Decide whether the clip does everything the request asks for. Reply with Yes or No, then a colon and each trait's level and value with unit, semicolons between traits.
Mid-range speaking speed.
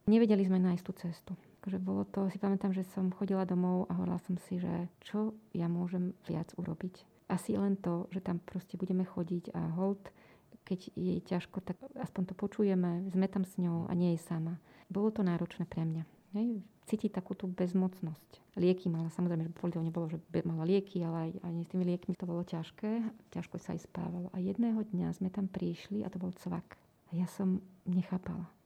No: fast, 195 wpm